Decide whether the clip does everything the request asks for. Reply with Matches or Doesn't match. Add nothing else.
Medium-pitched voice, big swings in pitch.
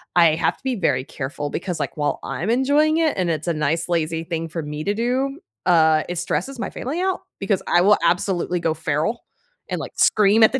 Matches